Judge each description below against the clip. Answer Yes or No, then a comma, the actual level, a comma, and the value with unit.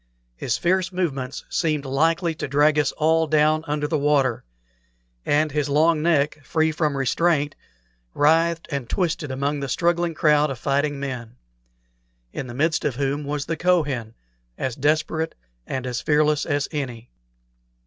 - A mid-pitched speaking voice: Yes, medium, 150 Hz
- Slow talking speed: No, average, 150 wpm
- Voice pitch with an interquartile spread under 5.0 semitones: Yes, narrow, 2.6 semitones